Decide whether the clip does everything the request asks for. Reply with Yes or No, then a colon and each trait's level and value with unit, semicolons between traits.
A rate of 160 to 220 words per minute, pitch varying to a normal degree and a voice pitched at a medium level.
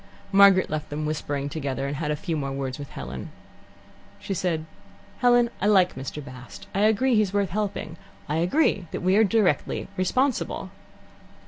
No: average, 175 wpm; wide, 6.0 semitones; medium, 170 Hz